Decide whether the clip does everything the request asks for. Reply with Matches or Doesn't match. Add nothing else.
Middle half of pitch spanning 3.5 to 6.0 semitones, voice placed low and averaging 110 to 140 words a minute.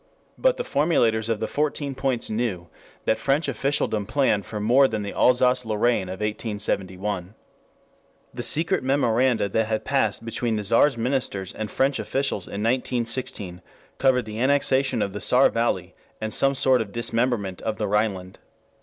Doesn't match